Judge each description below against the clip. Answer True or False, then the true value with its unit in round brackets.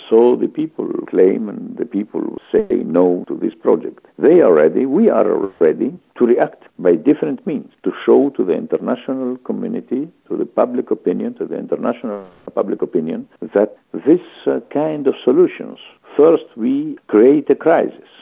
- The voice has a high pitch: True (320 Hz)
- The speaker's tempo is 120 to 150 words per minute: False (160 wpm)